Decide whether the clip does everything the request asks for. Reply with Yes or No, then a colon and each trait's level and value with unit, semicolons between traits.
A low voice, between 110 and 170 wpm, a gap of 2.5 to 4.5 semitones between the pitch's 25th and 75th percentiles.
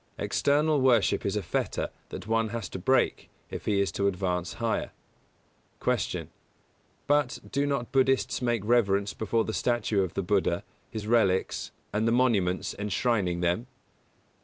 Yes: low, 110 Hz; average, 155 wpm; average, 4.0 semitones